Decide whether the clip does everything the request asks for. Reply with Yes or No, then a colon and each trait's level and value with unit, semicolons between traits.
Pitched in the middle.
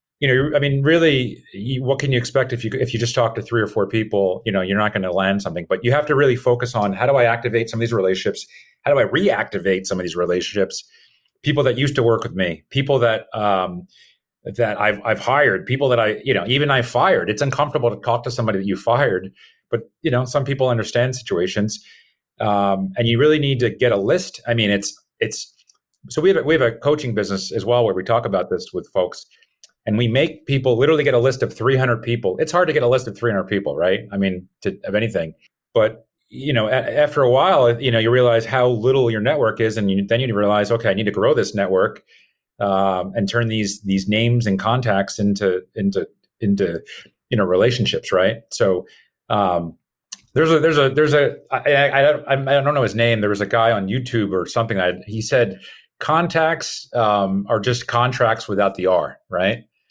No: low, 115 Hz